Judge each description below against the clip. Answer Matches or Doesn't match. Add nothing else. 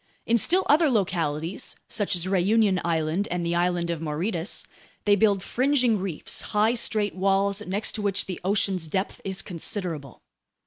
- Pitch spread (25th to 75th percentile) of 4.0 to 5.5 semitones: Doesn't match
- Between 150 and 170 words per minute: Matches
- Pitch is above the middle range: Matches